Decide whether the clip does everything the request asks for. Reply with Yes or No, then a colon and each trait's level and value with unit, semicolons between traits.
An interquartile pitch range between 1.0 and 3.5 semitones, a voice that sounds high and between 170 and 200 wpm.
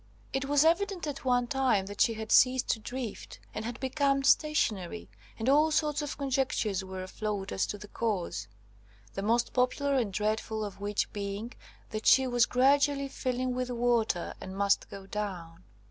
No: average, 4.9 semitones; high, 240 Hz; average, 175 wpm